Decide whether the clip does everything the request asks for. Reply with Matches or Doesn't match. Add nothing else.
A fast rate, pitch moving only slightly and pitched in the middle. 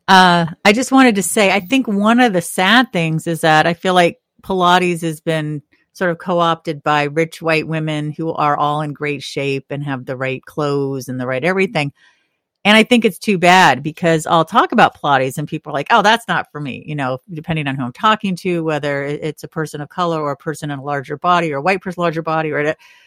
Doesn't match